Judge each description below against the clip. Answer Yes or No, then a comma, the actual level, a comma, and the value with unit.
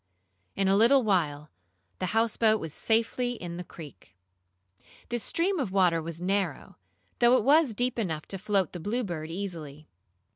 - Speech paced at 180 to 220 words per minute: No, average, 155 wpm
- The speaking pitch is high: Yes, high, 195 Hz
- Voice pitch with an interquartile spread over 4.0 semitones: Yes, wide, 5.6 semitones